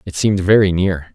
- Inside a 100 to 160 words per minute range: No, fast, 210 wpm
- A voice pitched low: Yes, very low, 95 Hz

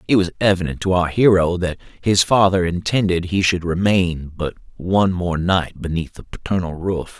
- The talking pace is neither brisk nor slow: Yes, average, 175 wpm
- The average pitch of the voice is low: Yes, very low, 90 Hz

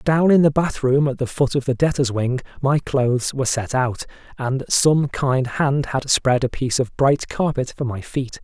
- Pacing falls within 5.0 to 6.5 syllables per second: No, 4.7 syllables/s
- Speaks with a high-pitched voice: No, low, 135 Hz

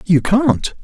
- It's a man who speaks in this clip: Yes, male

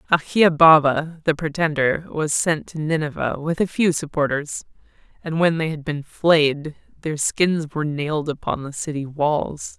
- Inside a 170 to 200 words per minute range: No, average, 155 wpm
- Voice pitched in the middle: Yes, medium, 155 Hz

